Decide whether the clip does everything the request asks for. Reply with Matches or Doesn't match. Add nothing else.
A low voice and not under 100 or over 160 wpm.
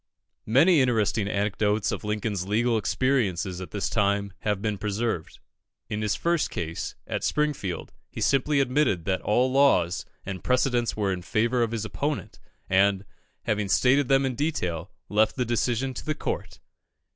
Matches